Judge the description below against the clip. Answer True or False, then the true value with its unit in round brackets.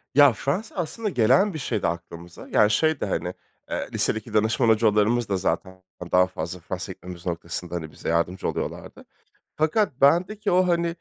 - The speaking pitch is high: False (110 Hz)